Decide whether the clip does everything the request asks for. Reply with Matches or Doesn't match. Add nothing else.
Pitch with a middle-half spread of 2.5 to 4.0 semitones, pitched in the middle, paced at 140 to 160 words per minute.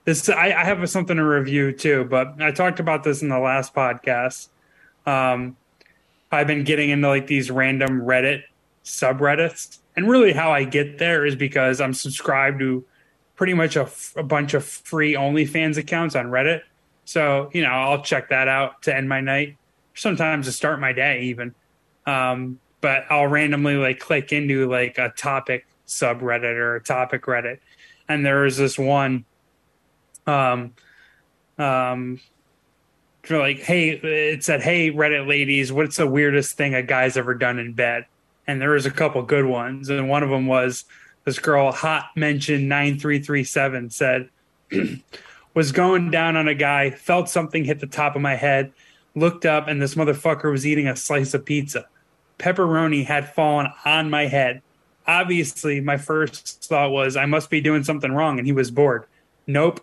Doesn't match